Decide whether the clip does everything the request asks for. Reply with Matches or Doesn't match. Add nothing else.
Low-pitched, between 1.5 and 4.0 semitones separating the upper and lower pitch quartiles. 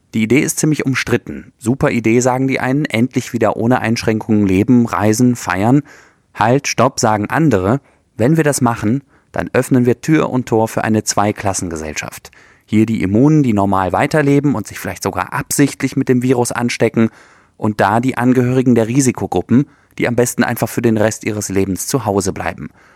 Matches